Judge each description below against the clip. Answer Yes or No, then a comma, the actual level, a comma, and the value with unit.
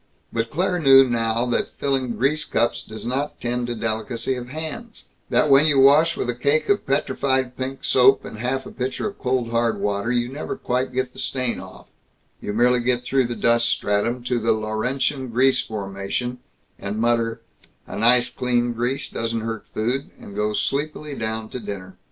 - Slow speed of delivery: No, average, 185 wpm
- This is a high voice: No, low, 125 Hz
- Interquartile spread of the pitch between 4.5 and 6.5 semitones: No, average, 2.7 semitones